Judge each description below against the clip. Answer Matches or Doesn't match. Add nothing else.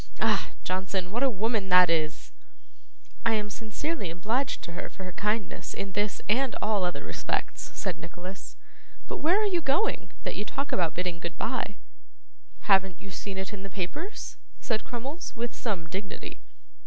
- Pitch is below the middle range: Doesn't match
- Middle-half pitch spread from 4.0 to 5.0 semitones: Matches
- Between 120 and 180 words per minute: Matches